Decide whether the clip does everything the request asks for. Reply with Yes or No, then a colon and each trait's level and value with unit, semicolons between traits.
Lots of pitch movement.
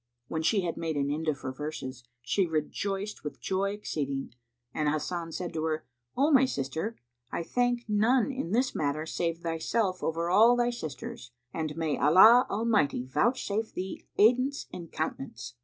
Yes: wide, 6.2 semitones